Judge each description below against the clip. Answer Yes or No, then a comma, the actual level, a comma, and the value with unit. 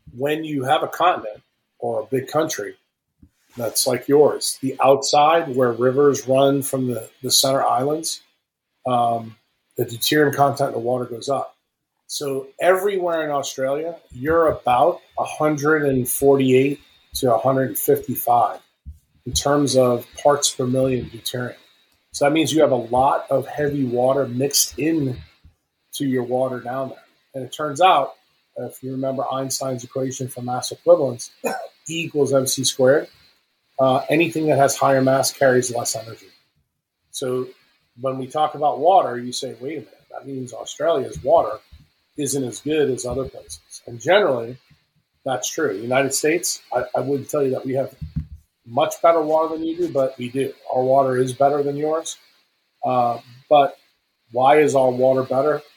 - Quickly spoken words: No, average, 155 wpm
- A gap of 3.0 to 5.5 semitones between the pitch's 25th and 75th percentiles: No, narrow, 2.5 semitones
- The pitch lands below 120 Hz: No, low, 135 Hz